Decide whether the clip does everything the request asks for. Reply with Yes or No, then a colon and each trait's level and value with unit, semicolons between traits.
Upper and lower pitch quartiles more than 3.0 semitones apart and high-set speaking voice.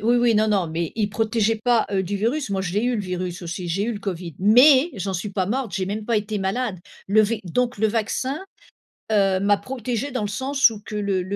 Yes: average, 3.6 semitones; high, 210 Hz